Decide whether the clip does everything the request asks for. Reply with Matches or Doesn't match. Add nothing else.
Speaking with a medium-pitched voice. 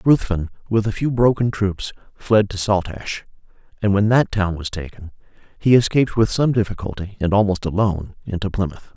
Doesn't match